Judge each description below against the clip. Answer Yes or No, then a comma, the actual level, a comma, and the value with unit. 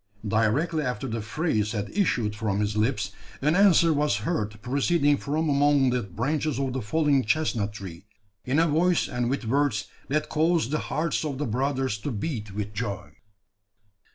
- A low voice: Yes, low, 130 Hz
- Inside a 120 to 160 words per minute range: No, average, 170 wpm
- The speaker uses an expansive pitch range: Yes, wide, 6.1 semitones